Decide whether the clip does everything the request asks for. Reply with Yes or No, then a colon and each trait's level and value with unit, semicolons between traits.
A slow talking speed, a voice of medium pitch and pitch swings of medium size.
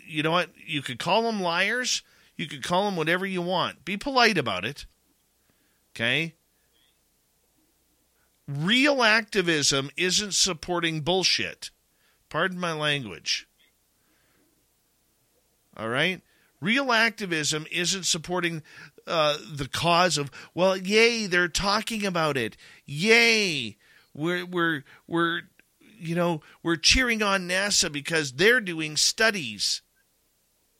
Yes: slow, 115 wpm; medium, 175 Hz; average, 4.5 semitones